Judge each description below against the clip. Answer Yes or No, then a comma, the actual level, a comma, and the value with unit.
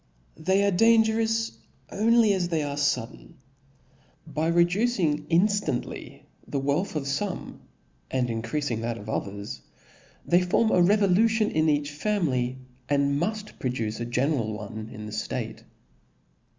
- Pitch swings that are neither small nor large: No, wide, 8.2 semitones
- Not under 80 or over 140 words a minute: Yes, slow, 135 wpm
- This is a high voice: No, medium, 155 Hz